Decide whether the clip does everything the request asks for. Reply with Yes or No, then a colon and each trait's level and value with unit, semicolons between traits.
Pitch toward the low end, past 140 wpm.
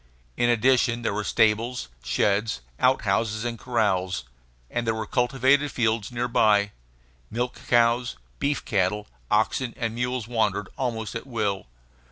No: low, 115 Hz; slow, 135 wpm